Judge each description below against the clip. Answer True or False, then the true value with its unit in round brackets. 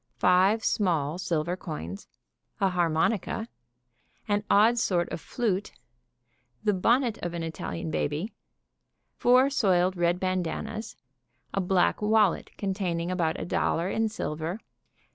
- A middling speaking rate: False (120 wpm)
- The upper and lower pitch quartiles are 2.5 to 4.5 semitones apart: True (3.9 semitones)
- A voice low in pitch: False (185 Hz)